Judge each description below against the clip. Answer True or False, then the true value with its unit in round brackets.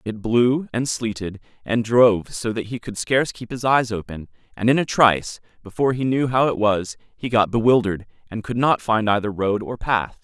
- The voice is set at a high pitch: False (115 Hz)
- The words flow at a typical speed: False (210 wpm)